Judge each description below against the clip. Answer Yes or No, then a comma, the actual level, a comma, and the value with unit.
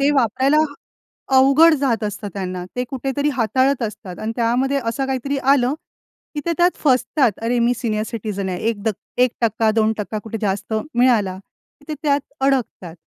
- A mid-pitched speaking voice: No, high, 240 Hz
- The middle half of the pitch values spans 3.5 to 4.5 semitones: Yes, average, 4.0 semitones